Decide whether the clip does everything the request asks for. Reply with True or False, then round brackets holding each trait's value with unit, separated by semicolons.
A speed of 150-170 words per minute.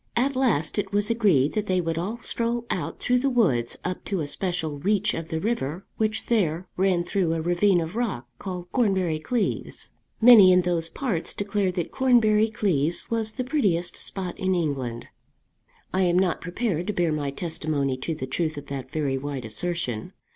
False (185 wpm)